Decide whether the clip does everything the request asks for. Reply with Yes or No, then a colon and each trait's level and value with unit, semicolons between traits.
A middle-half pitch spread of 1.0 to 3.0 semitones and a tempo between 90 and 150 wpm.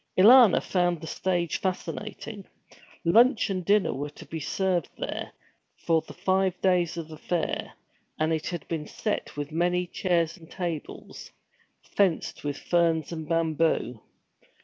Yes: average, 2.7 semitones; average, 145 wpm